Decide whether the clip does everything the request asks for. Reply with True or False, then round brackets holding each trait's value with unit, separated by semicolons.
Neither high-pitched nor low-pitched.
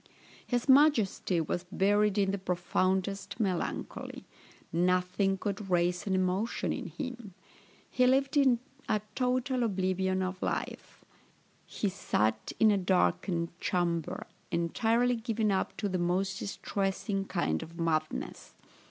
False (195 Hz)